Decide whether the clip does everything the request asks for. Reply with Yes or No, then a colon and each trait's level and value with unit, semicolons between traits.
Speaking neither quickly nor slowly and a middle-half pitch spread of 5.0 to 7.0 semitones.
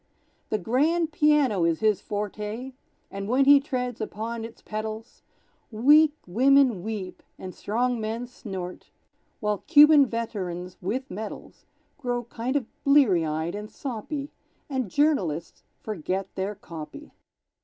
No: slow, 125 wpm; wide, 5.4 semitones